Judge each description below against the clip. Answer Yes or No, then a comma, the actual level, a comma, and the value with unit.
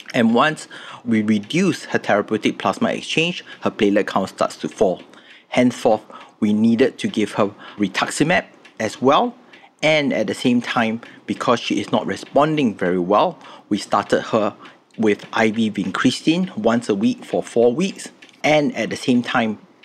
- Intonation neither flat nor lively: No, wide, 8.1 semitones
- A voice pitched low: Yes, low, 120 Hz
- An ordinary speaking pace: Yes, average, 155 wpm